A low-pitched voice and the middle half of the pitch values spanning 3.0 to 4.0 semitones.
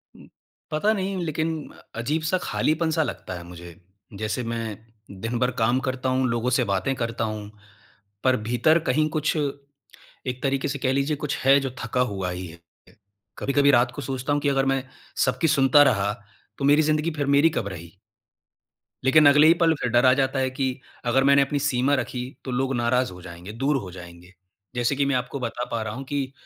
Yes: low, 130 Hz; average, 3.6 semitones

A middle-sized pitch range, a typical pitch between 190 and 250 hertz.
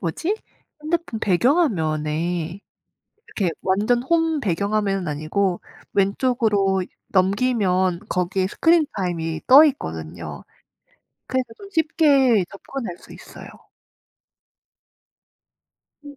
No: wide, 7.2 semitones; high, 200 Hz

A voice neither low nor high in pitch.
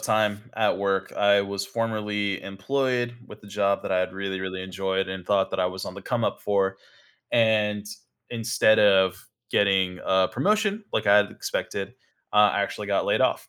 No: low, 100 Hz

